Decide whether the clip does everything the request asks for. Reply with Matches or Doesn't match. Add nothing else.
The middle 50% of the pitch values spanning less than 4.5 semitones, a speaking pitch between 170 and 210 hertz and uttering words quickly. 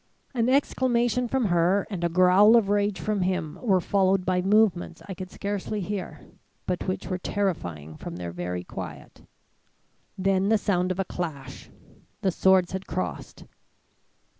Doesn't match